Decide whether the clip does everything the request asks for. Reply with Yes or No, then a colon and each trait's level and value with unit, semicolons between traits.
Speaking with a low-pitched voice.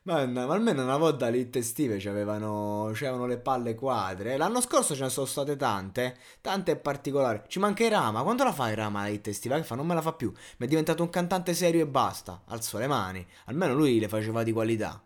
Yes: low, 130 Hz